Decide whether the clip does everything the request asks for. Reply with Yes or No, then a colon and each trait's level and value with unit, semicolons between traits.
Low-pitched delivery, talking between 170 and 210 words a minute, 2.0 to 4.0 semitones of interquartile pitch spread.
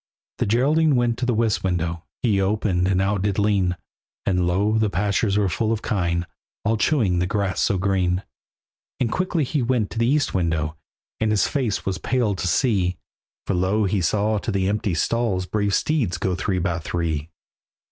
Yes: low, 100 Hz; average, 190 wpm; average, 3.7 semitones